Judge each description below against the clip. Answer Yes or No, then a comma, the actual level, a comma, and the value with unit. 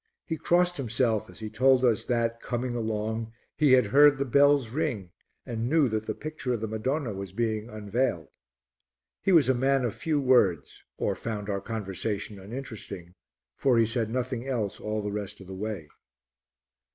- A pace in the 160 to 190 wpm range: Yes, average, 175 wpm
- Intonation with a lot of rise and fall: No, average, 3.8 semitones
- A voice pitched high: No, low, 115 Hz